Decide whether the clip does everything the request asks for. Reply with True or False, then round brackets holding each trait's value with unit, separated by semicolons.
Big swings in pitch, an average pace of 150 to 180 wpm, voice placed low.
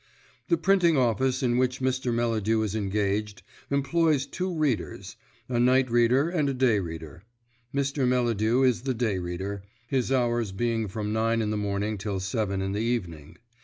False (4.1 semitones; 165 wpm; 115 Hz)